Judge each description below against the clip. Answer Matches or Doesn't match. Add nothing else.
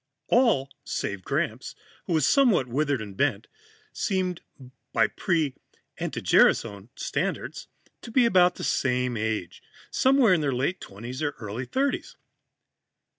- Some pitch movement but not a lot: Doesn't match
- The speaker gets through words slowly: Matches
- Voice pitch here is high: Doesn't match